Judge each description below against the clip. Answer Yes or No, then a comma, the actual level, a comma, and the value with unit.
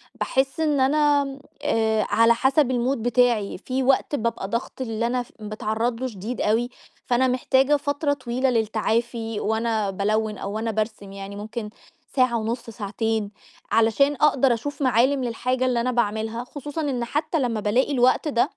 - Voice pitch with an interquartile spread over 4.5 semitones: No, average, 3.1 semitones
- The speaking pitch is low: No, high, 235 Hz